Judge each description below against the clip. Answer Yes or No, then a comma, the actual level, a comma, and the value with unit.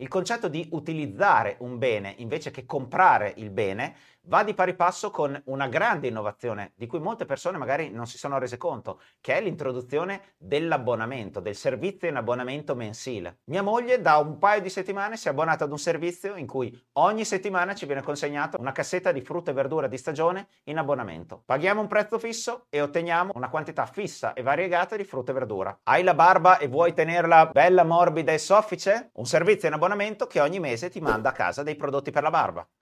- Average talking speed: No, fast, 200 wpm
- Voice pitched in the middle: Yes, medium, 160 Hz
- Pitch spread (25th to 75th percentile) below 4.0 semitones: No, wide, 5.6 semitones